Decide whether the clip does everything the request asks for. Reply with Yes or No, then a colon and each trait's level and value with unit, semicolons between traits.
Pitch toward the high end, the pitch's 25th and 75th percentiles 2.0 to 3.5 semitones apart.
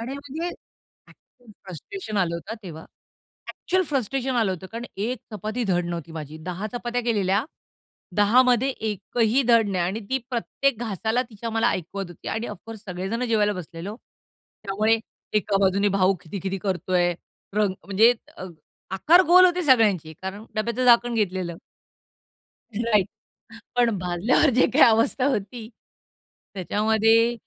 No: high, 215 Hz; average, 4.2 semitones